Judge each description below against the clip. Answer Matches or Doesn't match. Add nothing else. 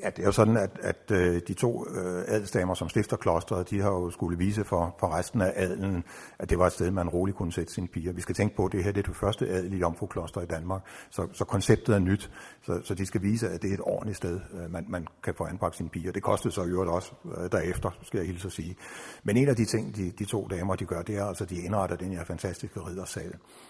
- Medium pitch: Doesn't match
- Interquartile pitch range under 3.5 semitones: Matches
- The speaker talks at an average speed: Doesn't match